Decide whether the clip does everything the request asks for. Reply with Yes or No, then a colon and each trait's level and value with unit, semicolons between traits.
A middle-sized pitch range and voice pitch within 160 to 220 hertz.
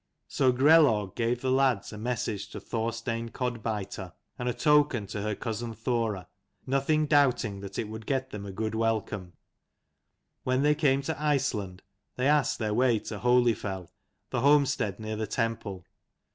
No: average, 3.7 semitones; low, 115 Hz